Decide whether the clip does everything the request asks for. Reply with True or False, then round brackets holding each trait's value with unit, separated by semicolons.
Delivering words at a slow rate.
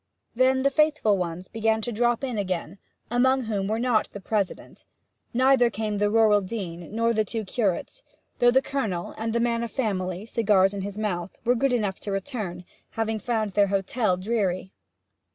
False (175 wpm)